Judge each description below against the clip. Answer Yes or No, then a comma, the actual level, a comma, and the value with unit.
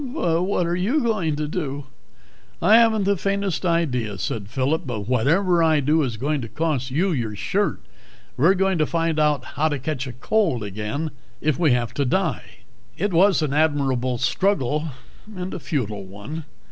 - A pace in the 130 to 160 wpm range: No, average, 175 wpm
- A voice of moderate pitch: Yes, medium, 155 Hz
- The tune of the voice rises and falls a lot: Yes, wide, 5.8 semitones